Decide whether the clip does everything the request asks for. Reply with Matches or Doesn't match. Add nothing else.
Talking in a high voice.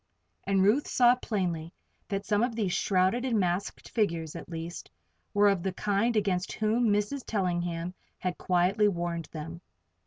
Matches